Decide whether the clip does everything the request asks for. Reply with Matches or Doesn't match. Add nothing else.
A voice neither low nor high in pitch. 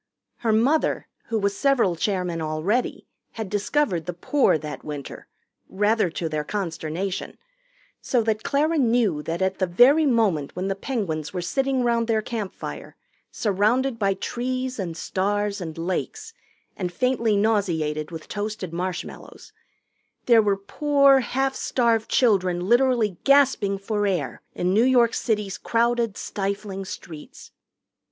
Doesn't match